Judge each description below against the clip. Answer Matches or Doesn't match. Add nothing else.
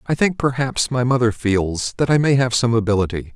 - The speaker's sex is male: Matches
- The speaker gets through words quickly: Matches